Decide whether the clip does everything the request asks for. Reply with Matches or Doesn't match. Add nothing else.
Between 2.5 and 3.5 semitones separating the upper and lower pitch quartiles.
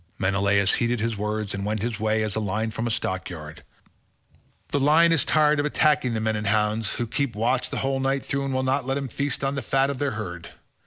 Doesn't match